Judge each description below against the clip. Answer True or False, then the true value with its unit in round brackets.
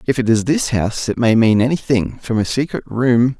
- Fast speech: True (230 wpm)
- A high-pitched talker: False (120 Hz)